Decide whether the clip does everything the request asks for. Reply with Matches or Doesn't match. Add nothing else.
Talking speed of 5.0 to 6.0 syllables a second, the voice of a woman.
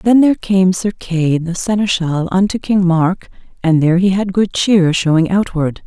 Doesn't match